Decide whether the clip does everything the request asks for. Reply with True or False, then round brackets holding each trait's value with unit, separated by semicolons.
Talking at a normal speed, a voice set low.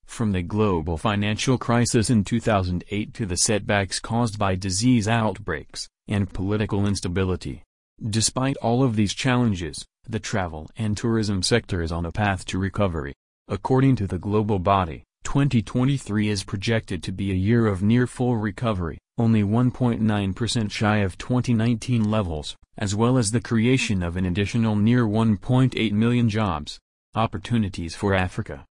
True (145 wpm; 105 Hz)